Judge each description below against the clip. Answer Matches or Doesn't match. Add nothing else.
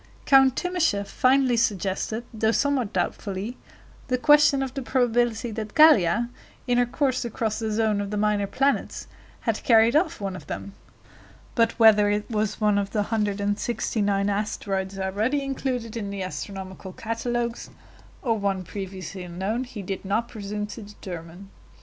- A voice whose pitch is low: Doesn't match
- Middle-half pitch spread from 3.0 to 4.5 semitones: Matches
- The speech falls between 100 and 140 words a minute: Doesn't match